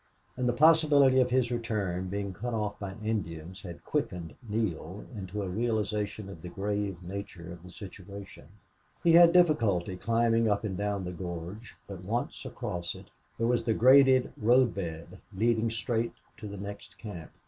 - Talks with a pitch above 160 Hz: No, low, 105 Hz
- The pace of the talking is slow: No, average, 170 wpm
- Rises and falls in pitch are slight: No, average, 4.0 semitones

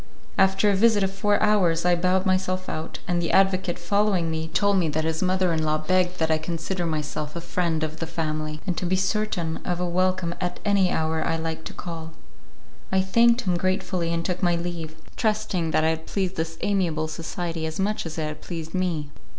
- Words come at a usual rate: No, fast, 215 wpm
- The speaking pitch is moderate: Yes, medium, 175 Hz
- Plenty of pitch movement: No, average, 2.7 semitones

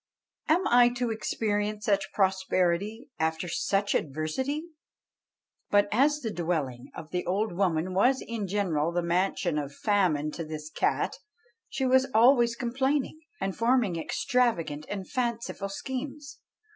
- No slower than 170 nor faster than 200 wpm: No, slow, 135 wpm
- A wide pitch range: Yes, wide, 6.2 semitones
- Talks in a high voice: Yes, high, 205 Hz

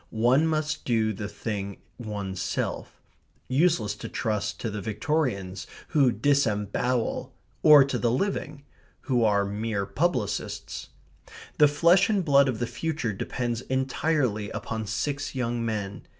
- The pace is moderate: No, slow, 130 wpm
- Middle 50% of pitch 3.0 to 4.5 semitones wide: No, wide, 5.5 semitones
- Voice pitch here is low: Yes, low, 120 Hz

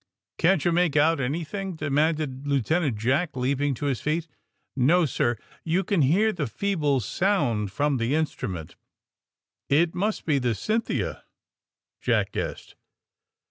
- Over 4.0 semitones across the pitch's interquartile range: Yes, average, 4.6 semitones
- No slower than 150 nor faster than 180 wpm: No, average, 140 wpm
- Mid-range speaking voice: Yes, medium, 150 Hz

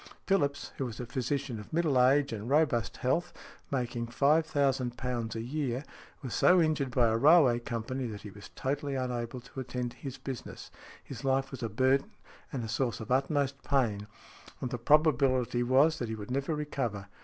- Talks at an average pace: Yes, average, 180 wpm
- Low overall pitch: Yes, low, 130 Hz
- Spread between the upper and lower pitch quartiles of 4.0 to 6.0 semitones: No, average, 3.0 semitones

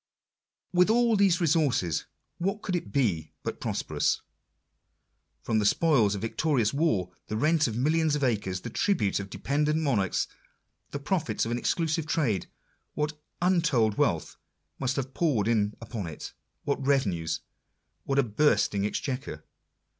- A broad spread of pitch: Yes, wide, 7.1 semitones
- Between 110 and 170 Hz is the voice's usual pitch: Yes, low, 135 Hz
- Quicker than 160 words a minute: No, average, 145 wpm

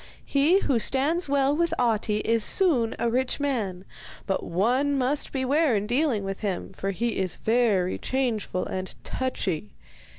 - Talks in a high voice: Yes, high, 240 Hz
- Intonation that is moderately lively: No, wide, 5.8 semitones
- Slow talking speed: No, average, 155 wpm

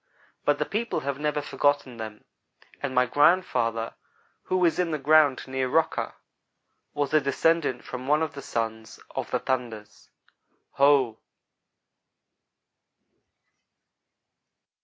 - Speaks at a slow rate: Yes, slow, 115 wpm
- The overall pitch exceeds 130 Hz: Yes, medium, 140 Hz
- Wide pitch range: No, average, 3.7 semitones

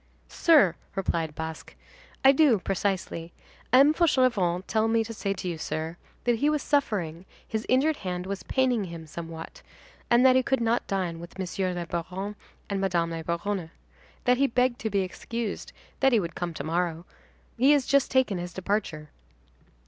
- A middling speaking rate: Yes, average, 175 wpm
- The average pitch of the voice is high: Yes, high, 195 Hz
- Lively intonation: Yes, wide, 6.4 semitones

